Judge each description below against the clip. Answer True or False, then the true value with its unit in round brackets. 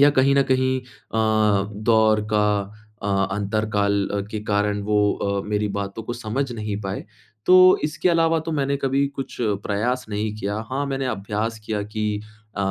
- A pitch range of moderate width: True (4.4 semitones)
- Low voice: True (110 Hz)